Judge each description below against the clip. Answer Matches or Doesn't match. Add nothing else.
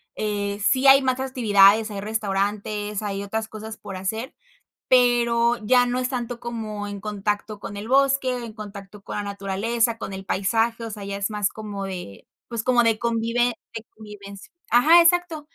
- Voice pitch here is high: Matches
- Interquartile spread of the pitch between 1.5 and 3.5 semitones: Matches